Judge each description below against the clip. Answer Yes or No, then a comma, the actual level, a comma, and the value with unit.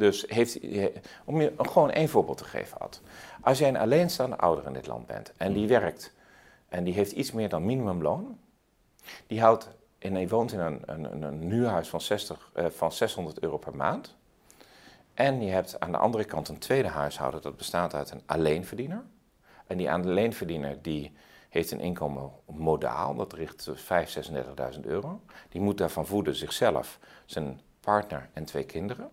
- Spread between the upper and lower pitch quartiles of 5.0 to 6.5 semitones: Yes, wide, 5.6 semitones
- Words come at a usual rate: Yes, average, 165 wpm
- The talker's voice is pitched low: Yes, very low, 85 Hz